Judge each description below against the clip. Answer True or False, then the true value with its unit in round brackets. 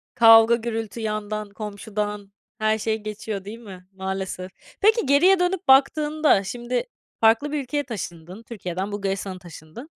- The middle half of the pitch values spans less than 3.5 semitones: False (3.8 semitones)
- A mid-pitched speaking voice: False (215 Hz)